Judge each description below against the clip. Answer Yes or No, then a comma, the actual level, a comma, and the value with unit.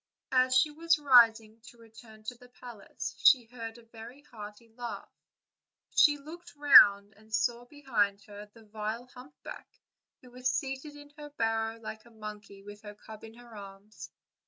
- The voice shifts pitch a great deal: No, average, 3.0 semitones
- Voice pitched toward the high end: Yes, high, 230 Hz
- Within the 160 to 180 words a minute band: Yes, average, 165 wpm